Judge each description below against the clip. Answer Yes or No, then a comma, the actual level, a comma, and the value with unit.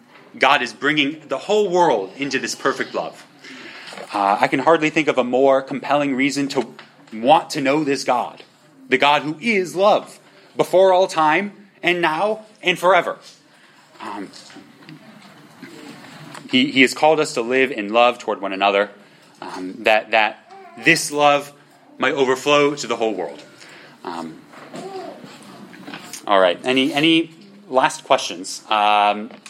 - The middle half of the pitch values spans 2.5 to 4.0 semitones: No, wide, 5.4 semitones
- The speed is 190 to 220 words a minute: No, average, 140 wpm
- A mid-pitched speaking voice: Yes, medium, 145 Hz